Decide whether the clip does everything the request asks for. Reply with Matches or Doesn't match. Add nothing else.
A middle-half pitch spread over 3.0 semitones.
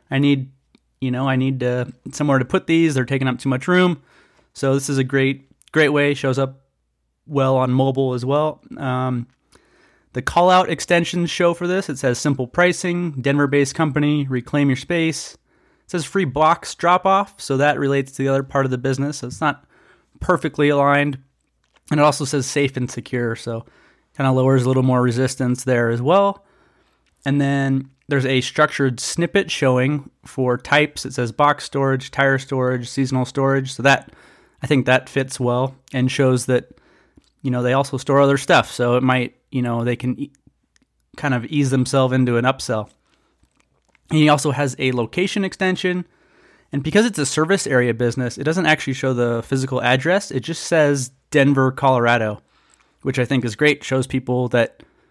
Doesn't match